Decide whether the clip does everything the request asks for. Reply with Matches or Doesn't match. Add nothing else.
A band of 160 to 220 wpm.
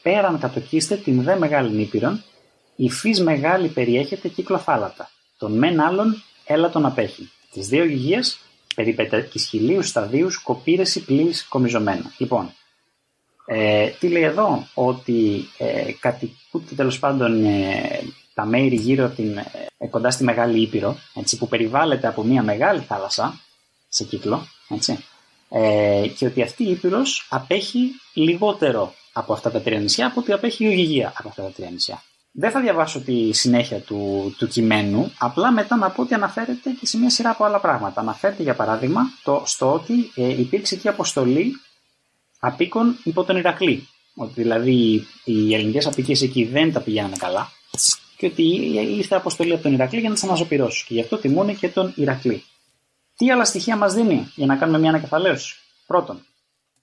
Matches